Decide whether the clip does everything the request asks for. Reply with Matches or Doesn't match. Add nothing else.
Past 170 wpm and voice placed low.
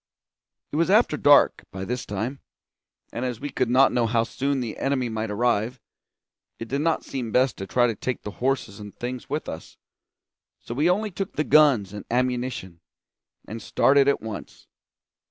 Matches